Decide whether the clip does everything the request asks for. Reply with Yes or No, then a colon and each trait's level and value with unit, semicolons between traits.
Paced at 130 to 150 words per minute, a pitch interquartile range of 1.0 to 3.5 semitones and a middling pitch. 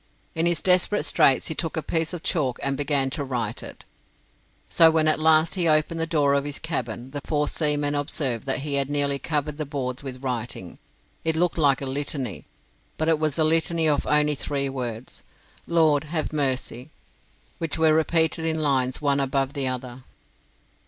No: average, 185 wpm; average, 2.9 semitones; medium, 145 Hz